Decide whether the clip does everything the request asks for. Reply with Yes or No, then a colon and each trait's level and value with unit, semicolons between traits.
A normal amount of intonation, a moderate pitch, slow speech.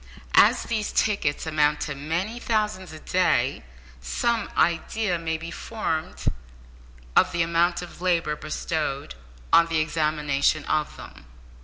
Yes: average, 3.2 semitones; medium, 165 Hz; slow, 130 wpm